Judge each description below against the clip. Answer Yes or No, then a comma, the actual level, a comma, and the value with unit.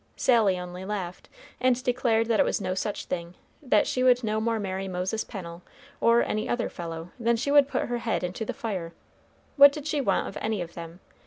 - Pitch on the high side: Yes, high, 215 Hz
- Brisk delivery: Yes, fast, 215 wpm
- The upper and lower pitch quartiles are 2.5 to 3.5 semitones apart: No, average, 4.8 semitones